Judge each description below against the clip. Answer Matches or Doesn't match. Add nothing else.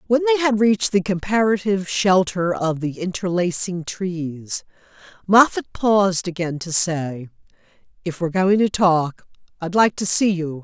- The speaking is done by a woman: Matches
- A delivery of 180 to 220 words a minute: Doesn't match